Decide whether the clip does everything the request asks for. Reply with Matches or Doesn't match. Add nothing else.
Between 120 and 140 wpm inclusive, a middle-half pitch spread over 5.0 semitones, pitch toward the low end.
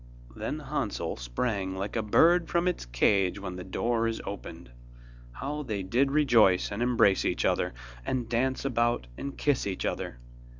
Doesn't match